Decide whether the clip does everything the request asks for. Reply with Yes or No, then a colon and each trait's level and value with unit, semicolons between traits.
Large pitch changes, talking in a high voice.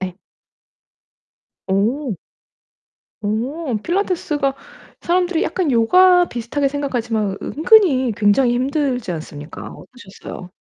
Yes: wide, 6.4 semitones; very high, 255 Hz